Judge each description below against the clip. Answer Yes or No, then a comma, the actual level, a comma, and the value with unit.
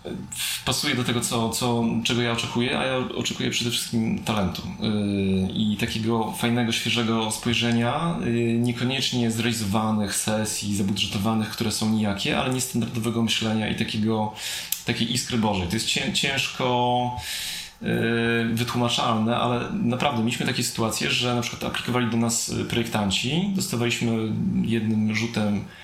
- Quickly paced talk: No, average, 130 wpm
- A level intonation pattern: Yes, narrow, 1.7 semitones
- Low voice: Yes, low, 115 Hz